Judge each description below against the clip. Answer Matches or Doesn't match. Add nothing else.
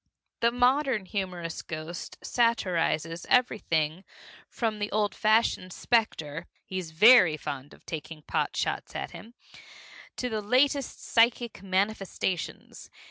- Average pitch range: Doesn't match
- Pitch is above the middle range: Matches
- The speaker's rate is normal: Doesn't match